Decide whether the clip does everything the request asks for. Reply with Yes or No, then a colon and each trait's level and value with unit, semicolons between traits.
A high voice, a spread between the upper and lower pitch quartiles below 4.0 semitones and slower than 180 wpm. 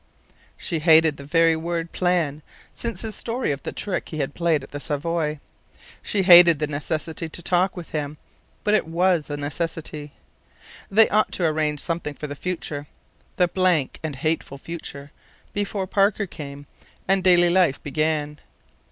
No: medium, 165 Hz; average, 3.2 semitones; average, 160 wpm